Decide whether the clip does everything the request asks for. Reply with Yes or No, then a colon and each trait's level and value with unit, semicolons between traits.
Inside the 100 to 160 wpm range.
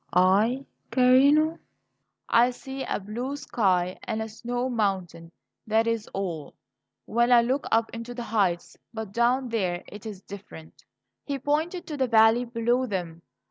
Yes: average, 150 wpm